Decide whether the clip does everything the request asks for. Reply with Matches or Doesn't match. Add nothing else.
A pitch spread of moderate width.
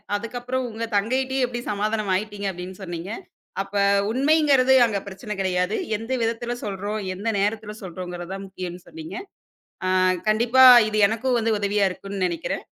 Matches